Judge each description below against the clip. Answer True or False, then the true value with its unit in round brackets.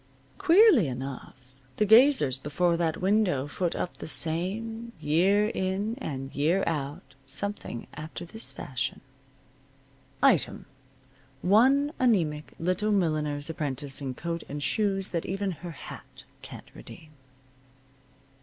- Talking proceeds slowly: True (115 wpm)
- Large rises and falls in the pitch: True (6.0 semitones)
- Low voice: False (170 Hz)